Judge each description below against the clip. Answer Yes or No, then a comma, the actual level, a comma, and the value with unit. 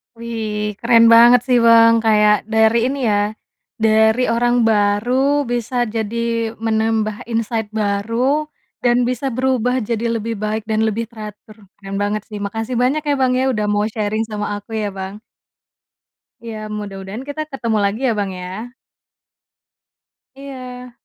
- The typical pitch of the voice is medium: No, high, 225 Hz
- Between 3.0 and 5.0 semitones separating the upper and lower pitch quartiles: No, narrow, 2.5 semitones